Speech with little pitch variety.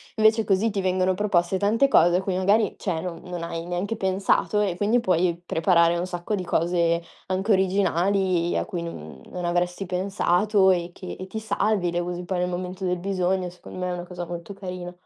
Yes: narrow, 2.0 semitones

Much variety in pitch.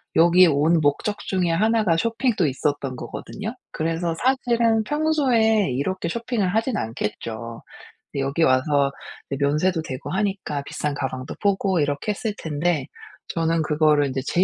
Yes: wide, 6.7 semitones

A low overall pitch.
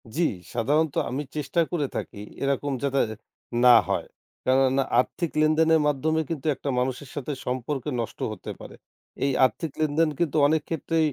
No: medium, 145 Hz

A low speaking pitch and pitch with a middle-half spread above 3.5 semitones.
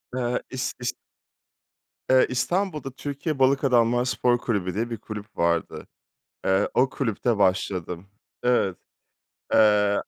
Yes: low, 120 Hz; average, 4.3 semitones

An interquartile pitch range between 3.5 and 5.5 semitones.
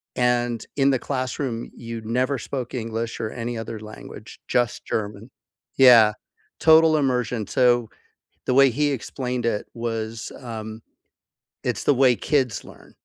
No: narrow, 2.5 semitones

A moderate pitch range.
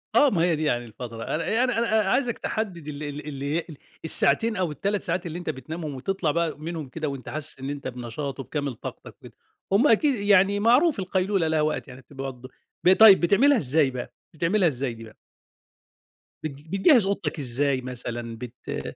No: wide, 6.6 semitones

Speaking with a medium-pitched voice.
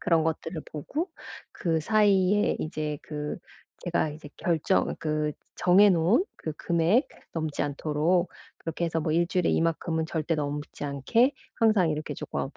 Yes: medium, 165 Hz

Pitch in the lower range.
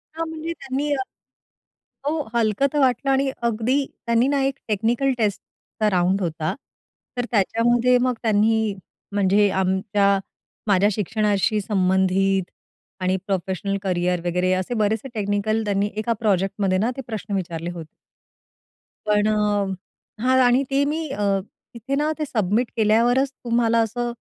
No: high, 215 Hz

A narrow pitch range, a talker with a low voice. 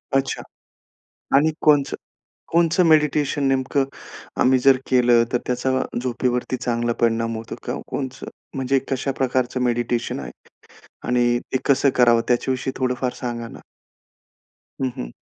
Yes: narrow, 1.9 semitones; low, 125 Hz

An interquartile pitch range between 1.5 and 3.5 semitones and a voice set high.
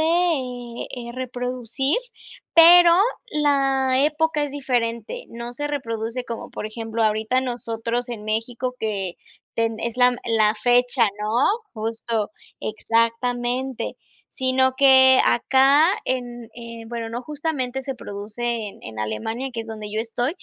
Yes: narrow, 2.6 semitones; high, 240 Hz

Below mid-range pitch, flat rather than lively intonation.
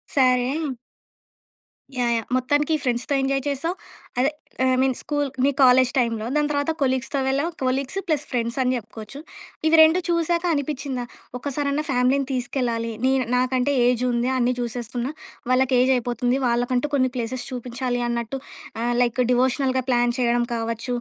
No: very high, 255 Hz; narrow, 2.3 semitones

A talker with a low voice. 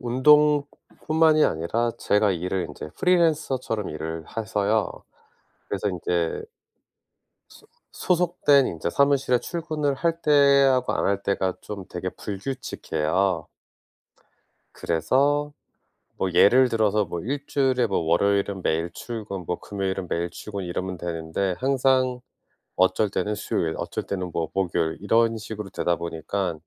Yes: low, 105 Hz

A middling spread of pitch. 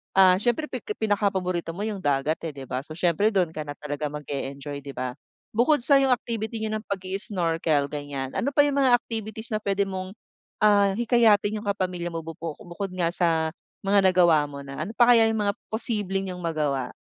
No: wide, 5.7 semitones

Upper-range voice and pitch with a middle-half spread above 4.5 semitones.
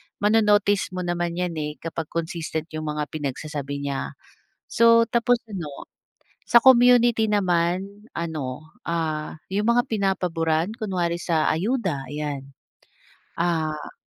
No: medium, 170 Hz; average, 5.0 semitones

